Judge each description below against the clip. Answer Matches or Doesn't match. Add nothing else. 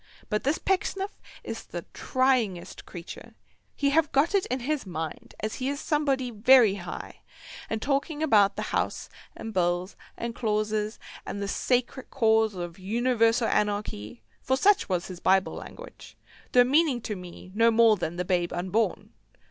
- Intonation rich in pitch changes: Matches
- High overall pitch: Matches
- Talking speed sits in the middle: Matches